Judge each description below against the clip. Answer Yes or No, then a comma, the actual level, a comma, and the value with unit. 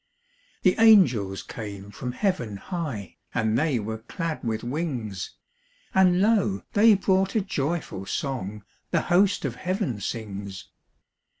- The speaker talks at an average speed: No, slow, 125 wpm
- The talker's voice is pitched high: No, low, 135 Hz